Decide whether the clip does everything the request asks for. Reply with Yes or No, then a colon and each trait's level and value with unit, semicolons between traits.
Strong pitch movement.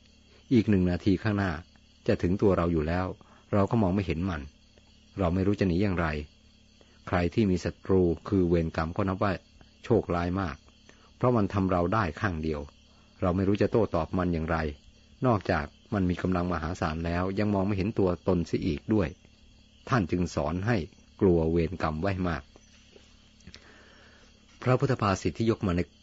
No: average, 3.9 semitones